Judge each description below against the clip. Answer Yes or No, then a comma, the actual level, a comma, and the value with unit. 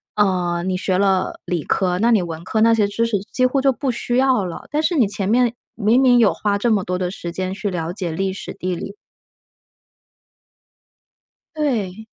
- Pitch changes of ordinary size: Yes, average, 4.5 semitones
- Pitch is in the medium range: No, high, 200 Hz